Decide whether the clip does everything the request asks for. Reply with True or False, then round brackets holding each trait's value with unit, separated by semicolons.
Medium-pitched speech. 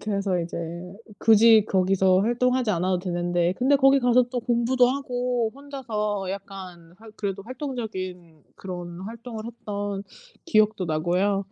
False (205 Hz)